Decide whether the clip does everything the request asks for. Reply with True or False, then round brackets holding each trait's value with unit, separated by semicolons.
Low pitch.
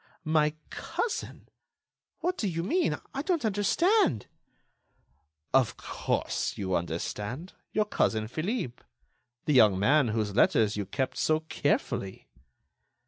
False (150 Hz)